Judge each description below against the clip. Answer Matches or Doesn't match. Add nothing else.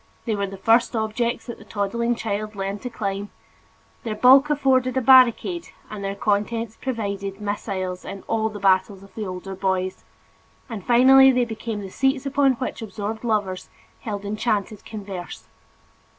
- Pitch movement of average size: Matches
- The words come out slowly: Doesn't match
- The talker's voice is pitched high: Matches